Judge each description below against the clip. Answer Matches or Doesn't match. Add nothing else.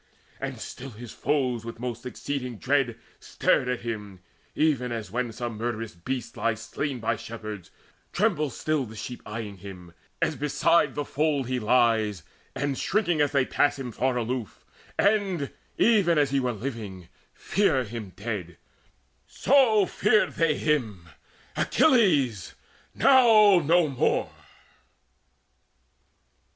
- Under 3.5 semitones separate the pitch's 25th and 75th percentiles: Doesn't match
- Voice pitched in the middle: Doesn't match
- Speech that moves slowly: Matches